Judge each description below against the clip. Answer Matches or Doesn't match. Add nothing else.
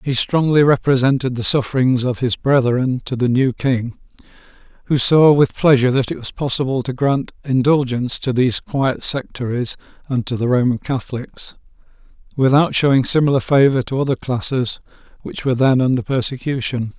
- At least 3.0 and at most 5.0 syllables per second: Doesn't match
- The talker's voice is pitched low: Matches